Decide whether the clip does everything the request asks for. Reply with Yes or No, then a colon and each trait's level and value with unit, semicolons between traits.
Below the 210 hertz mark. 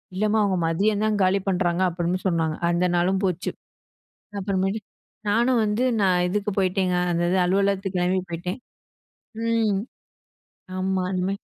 Yes: high, 190 Hz